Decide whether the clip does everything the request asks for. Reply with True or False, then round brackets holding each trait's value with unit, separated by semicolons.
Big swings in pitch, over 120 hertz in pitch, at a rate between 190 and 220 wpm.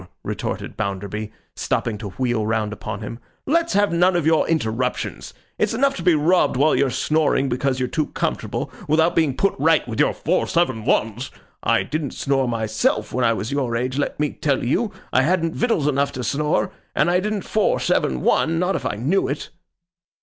True (6.1 semitones; 140 Hz; 195 wpm)